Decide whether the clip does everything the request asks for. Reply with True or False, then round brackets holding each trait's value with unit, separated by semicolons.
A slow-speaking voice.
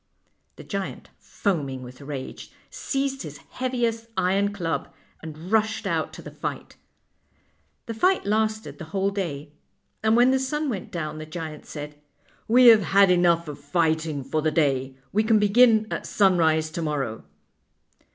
False (160 wpm)